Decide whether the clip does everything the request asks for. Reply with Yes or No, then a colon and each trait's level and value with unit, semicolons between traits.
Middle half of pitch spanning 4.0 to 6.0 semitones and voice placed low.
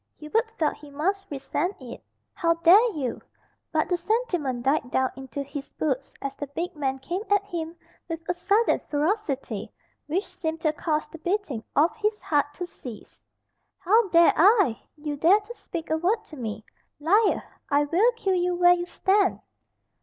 No: average, 5.2 semitones; very high, 330 Hz